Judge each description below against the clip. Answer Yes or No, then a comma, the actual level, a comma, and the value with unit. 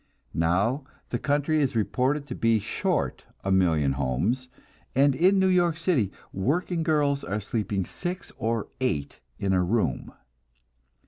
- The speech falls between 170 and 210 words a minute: No, average, 140 wpm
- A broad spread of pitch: Yes, wide, 7.5 semitones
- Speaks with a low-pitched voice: Yes, low, 125 Hz